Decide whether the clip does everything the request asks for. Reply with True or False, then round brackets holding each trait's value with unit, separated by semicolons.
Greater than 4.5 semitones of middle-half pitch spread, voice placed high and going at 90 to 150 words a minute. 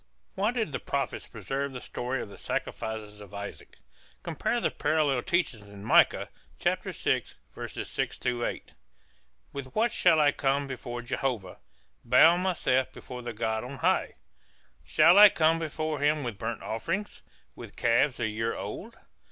False (5.6 semitones; 130 Hz; 145 wpm)